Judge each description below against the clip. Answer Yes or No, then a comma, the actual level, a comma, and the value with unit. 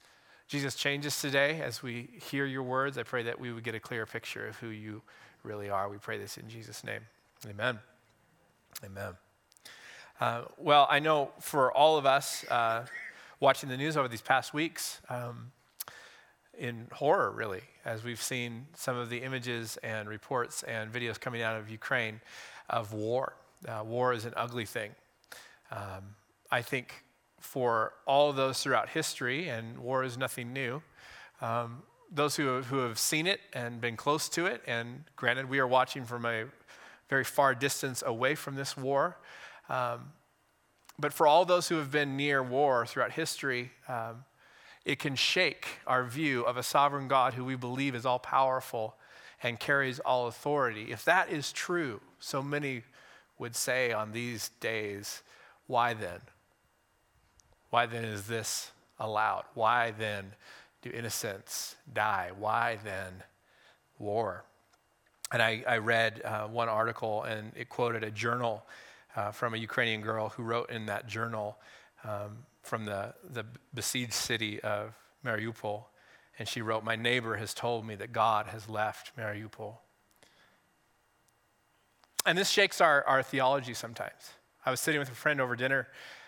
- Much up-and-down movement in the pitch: No, average, 3.4 semitones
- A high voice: No, low, 120 Hz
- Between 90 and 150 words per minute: No, average, 160 wpm